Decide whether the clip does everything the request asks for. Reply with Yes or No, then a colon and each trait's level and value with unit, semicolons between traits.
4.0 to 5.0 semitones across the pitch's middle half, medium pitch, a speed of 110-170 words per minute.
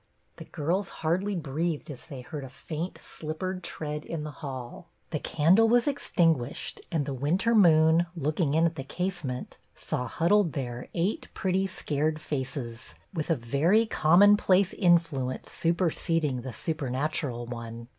Yes: average, 4.4 semitones; medium, 155 Hz; average, 145 wpm